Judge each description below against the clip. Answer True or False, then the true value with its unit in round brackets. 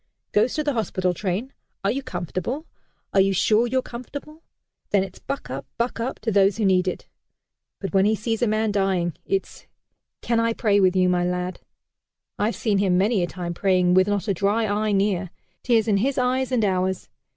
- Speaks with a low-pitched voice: False (205 Hz)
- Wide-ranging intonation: False (3.7 semitones)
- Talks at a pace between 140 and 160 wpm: False (200 wpm)